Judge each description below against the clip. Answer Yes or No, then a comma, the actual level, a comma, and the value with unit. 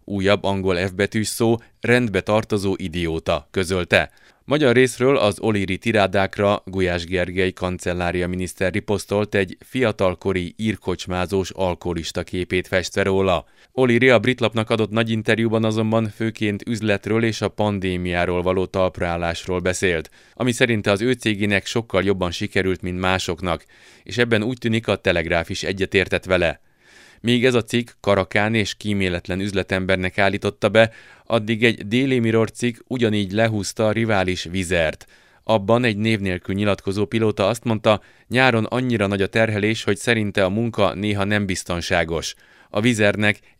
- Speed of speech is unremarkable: Yes, average, 140 wpm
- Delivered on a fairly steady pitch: No, average, 3.2 semitones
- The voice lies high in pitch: No, low, 100 Hz